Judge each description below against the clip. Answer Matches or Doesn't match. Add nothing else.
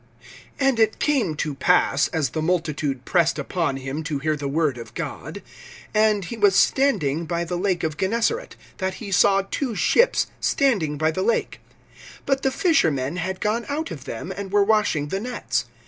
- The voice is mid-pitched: Matches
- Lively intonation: Matches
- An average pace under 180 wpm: Doesn't match